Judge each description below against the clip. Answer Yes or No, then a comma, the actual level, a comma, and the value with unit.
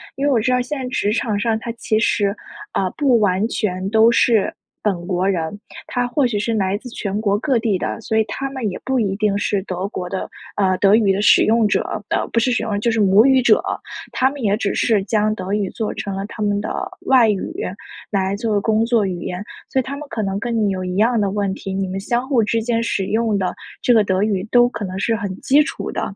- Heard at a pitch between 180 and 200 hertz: No, high, 215 Hz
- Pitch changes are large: No, average, 3.1 semitones